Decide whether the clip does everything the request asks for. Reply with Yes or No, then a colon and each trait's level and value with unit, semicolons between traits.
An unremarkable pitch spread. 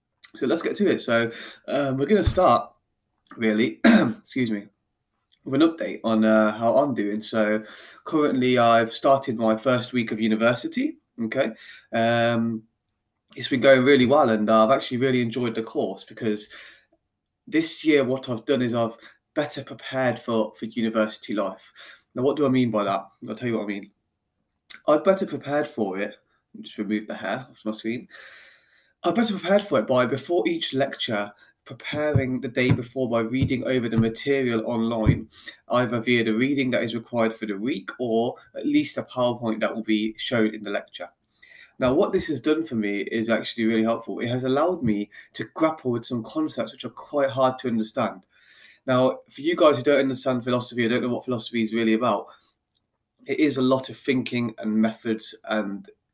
Yes: average, 3.4 semitones